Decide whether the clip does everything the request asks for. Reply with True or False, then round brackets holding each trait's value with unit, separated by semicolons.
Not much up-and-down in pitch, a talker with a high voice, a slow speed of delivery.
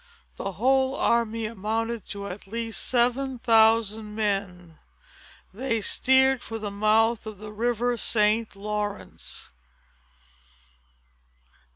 True (2.1 semitones; 220 Hz; 100 wpm)